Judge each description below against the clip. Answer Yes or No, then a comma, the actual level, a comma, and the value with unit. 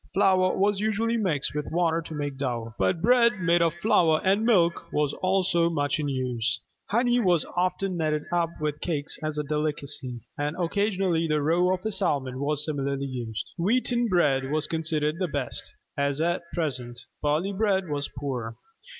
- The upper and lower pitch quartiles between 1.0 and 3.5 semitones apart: No, average, 4.4 semitones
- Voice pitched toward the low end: No, medium, 160 Hz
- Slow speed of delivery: No, average, 170 wpm